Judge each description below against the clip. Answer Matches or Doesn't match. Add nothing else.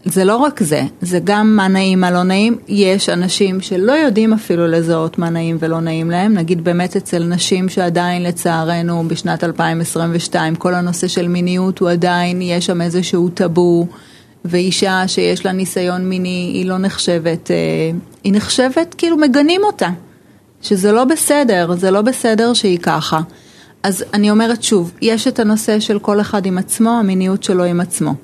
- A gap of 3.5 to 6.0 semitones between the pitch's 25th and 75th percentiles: Doesn't match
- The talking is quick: Matches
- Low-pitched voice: Doesn't match